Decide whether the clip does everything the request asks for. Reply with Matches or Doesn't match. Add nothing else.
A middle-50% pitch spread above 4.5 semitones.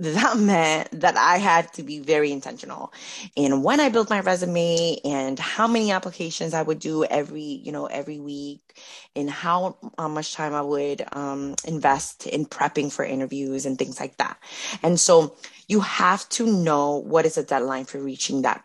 Doesn't match